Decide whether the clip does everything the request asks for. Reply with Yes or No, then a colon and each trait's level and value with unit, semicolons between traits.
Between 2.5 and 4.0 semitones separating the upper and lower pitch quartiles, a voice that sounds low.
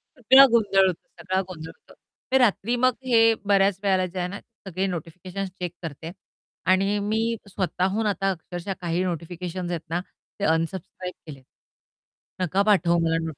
No: average, 2.8 semitones; medium, 185 Hz